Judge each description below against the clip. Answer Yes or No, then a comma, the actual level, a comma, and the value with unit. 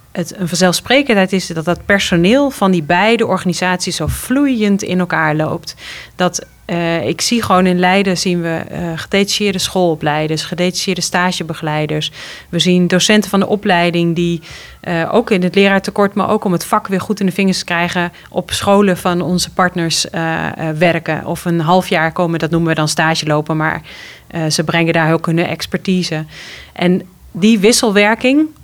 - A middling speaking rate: Yes, average, 170 wpm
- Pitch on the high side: No, medium, 180 Hz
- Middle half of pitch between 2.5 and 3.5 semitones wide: Yes, average, 2.8 semitones